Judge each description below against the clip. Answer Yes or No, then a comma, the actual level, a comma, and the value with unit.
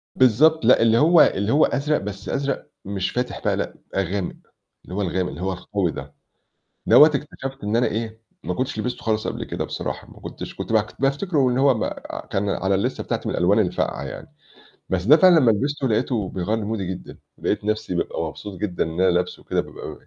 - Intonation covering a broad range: Yes, wide, 5.8 semitones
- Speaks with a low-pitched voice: Yes, low, 110 Hz